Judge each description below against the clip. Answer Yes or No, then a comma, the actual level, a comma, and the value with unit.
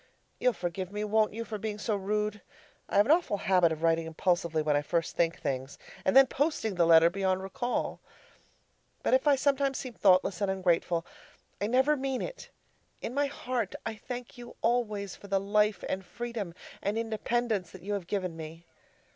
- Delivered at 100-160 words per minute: No, average, 190 wpm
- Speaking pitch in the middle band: No, high, 205 Hz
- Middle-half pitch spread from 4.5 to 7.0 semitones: Yes, average, 5.2 semitones